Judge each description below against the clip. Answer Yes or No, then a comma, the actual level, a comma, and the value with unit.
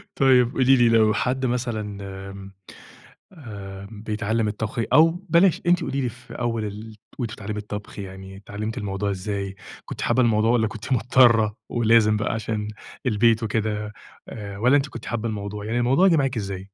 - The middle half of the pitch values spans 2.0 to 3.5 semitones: Yes, average, 3.0 semitones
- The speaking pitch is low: Yes, low, 110 Hz